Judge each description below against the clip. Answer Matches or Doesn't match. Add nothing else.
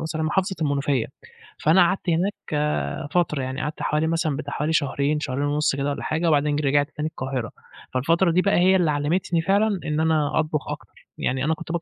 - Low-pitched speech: Doesn't match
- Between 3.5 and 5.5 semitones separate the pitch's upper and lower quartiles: Doesn't match